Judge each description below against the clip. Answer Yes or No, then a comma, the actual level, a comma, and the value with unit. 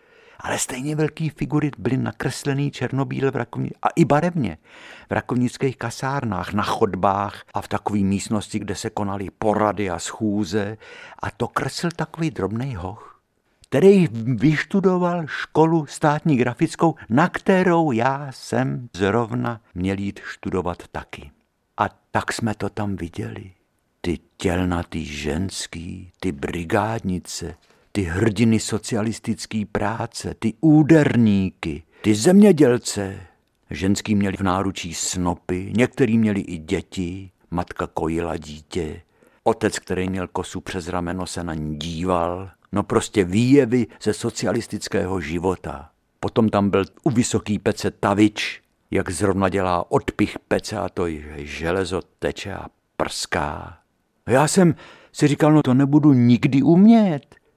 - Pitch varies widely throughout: Yes, wide, 6.3 semitones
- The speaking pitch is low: Yes, low, 105 Hz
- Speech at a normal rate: Yes, average, 125 wpm